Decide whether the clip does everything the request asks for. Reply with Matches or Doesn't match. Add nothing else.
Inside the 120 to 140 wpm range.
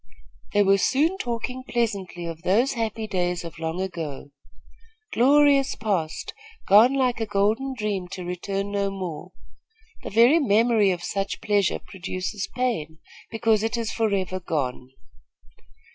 Matches